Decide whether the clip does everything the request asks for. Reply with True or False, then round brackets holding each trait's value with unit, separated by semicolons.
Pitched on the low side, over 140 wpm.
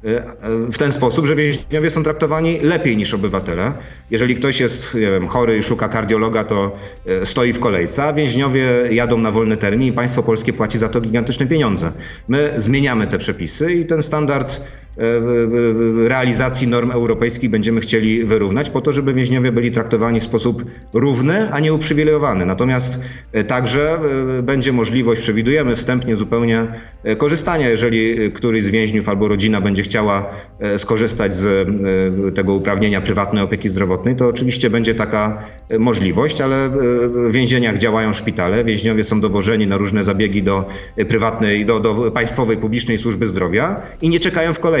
True (115 Hz; 155 wpm)